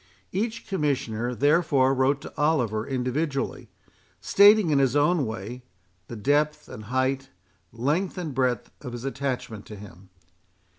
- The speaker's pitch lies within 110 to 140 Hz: Yes, low, 135 Hz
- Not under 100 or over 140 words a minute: Yes, slow, 135 wpm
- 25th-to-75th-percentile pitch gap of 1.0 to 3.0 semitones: No, average, 3.8 semitones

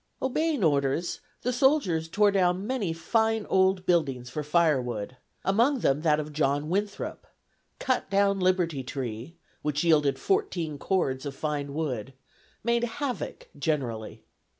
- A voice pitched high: No, medium, 165 Hz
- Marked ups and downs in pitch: Yes, wide, 6.4 semitones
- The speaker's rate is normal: No, slow, 130 wpm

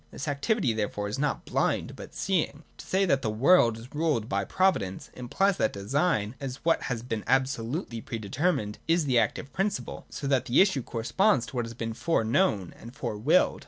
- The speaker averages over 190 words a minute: Yes, average, 200 wpm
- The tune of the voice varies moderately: No, wide, 6.4 semitones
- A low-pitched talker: Yes, low, 125 Hz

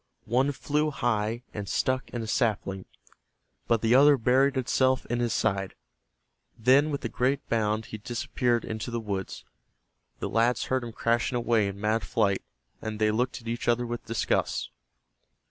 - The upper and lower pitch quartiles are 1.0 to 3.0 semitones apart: Yes, average, 2.7 semitones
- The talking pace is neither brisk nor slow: Yes, average, 165 wpm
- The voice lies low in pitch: Yes, low, 115 Hz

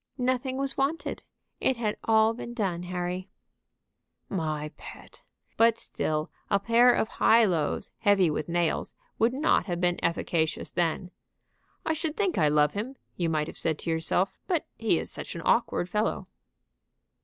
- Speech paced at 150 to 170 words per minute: Yes, average, 160 wpm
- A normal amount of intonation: No, wide, 6.1 semitones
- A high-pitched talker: Yes, high, 195 Hz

